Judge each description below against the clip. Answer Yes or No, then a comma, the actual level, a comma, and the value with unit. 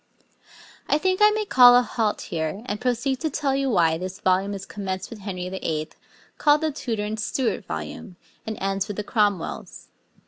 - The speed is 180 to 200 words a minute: Yes, average, 185 wpm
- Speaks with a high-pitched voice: Yes, high, 210 Hz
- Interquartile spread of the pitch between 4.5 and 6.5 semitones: Yes, wide, 5.5 semitones